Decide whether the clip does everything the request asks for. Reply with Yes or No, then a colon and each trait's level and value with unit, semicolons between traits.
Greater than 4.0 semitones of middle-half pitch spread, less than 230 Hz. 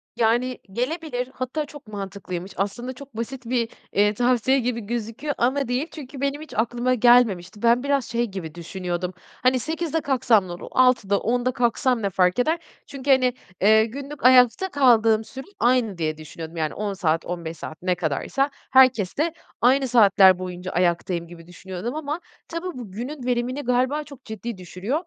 No: average, 5.3 semitones; high, 240 Hz